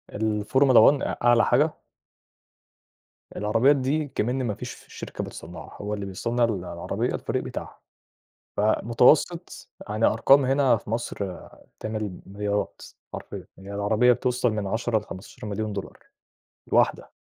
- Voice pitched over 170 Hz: No, low, 110 Hz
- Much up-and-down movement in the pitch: No, average, 3.3 semitones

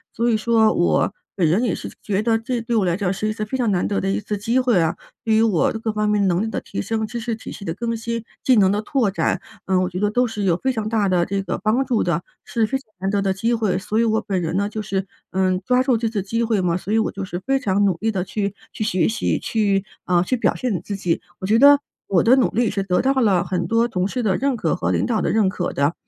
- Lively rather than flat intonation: No, average, 3.2 semitones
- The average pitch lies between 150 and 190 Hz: No, high, 210 Hz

